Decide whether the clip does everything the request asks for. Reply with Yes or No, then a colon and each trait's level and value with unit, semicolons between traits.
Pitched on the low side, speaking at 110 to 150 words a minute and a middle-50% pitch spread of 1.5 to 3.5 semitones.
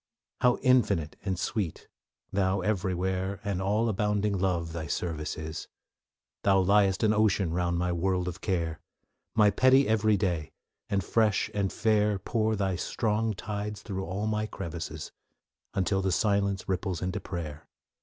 Yes: very low, 95 Hz; average, 145 wpm; average, 2.9 semitones